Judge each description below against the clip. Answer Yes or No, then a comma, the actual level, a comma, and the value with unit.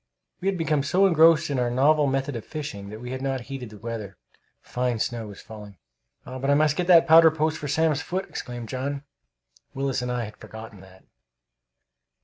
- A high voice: No, low, 135 Hz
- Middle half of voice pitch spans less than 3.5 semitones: No, average, 4.8 semitones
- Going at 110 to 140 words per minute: No, average, 195 wpm